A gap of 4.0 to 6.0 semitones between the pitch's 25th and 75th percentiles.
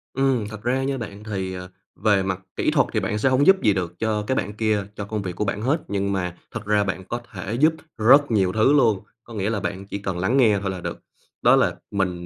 No: average, 3.5 semitones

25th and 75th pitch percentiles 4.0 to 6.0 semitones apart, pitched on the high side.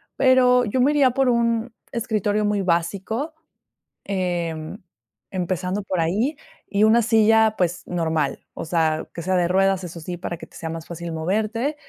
Yes: average, 4.9 semitones; high, 195 Hz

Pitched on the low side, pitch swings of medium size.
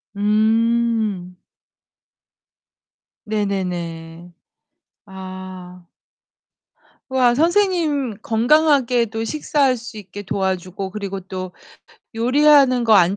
No: high, 215 Hz; average, 5.0 semitones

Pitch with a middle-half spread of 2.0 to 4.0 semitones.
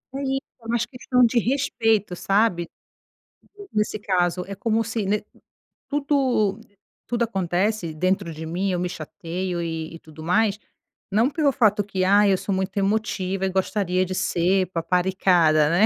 Yes: average, 3.6 semitones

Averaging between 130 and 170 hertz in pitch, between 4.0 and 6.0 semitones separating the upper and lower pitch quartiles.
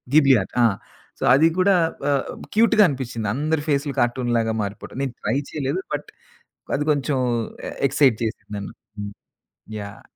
Yes: low, 135 Hz; average, 4.3 semitones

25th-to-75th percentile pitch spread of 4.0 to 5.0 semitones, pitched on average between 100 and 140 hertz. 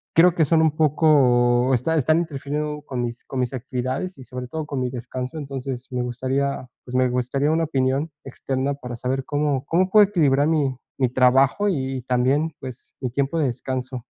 No: average, 3.1 semitones; low, 135 Hz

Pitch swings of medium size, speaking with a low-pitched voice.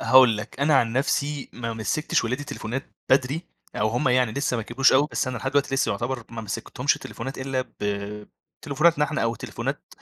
Yes: average, 3.5 semitones; low, 130 Hz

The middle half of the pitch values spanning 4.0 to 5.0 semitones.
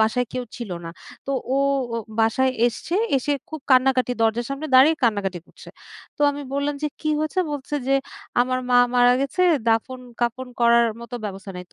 No: average, 2.8 semitones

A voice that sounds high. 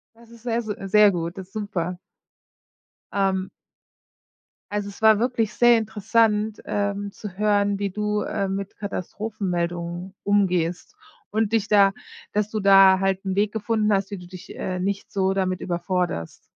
Yes: high, 200 Hz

